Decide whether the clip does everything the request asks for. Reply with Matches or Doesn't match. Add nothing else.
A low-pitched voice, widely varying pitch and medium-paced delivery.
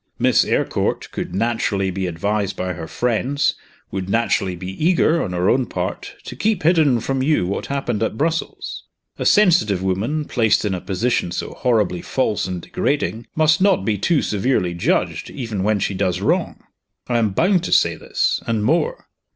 Matches